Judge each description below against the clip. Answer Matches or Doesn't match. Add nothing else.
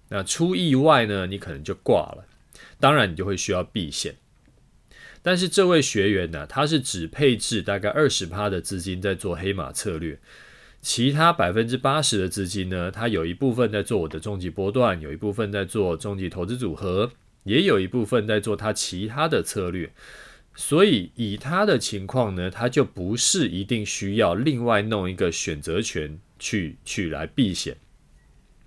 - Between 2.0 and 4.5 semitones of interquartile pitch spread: Doesn't match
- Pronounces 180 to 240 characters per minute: Doesn't match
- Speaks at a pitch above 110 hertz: Doesn't match